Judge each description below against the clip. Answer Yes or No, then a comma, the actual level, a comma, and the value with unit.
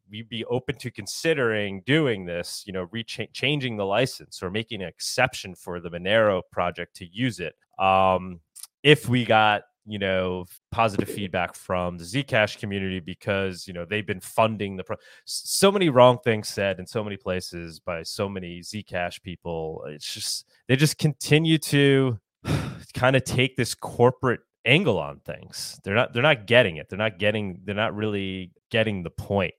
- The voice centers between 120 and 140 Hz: No, low, 105 Hz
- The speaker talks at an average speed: Yes, average, 175 wpm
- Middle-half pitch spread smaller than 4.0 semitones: No, average, 5.0 semitones